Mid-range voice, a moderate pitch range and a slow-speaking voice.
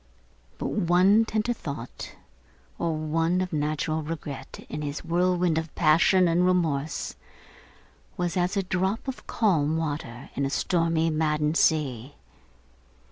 Yes: medium, 165 Hz; average, 3.1 semitones; slow, 130 wpm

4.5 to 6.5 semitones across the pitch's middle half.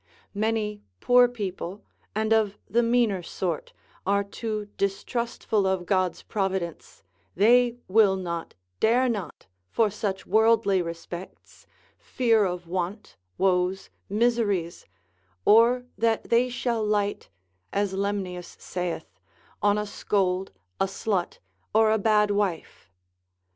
No: average, 2.9 semitones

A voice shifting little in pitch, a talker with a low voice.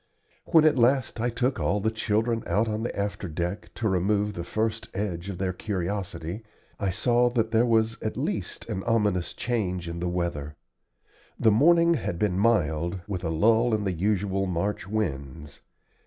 No: average, 4.1 semitones; low, 105 Hz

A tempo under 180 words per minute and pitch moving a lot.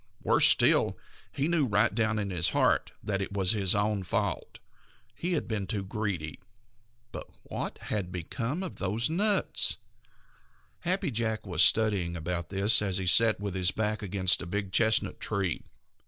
No: average, 165 wpm; average, 3.2 semitones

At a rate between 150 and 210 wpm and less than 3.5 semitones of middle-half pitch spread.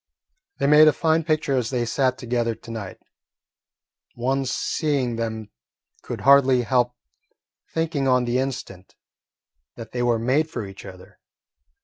No: average, 140 wpm; average, 3.1 semitones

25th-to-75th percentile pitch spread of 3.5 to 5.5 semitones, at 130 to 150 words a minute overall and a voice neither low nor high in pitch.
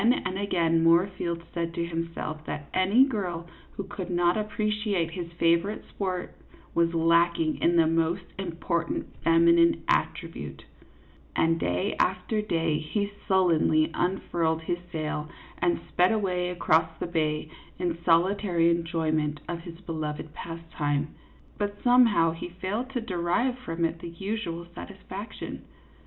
No: narrow, 2.4 semitones; slow, 135 wpm; medium, 170 Hz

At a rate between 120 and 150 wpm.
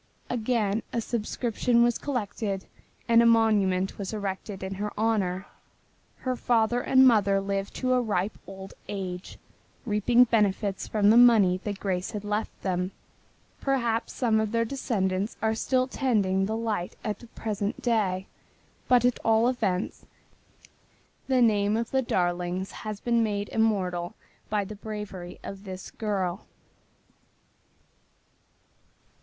Yes: slow, 135 wpm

